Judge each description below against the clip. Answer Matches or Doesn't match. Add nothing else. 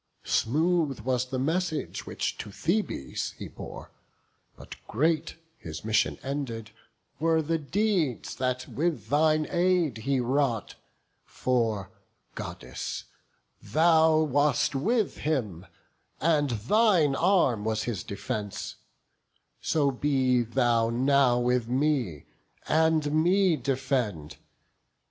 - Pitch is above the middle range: Doesn't match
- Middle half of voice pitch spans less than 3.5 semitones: Doesn't match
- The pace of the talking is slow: Matches